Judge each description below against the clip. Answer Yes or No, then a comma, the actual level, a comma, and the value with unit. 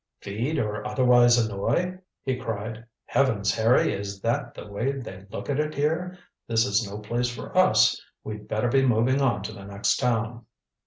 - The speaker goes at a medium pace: Yes, average, 175 wpm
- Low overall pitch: Yes, low, 115 Hz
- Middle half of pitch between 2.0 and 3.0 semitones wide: No, average, 3.8 semitones